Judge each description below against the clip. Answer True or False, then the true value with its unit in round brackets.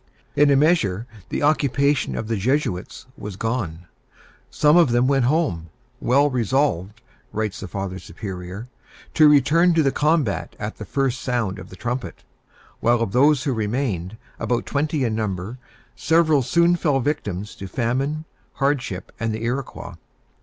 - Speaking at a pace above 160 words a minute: False (155 wpm)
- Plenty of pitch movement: True (5.8 semitones)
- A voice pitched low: True (125 Hz)